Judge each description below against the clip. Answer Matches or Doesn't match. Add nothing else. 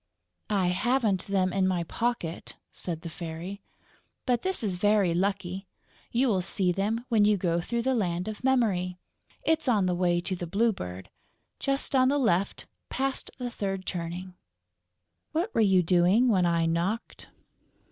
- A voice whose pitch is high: Matches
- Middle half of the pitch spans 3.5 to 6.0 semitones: Matches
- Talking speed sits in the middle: Matches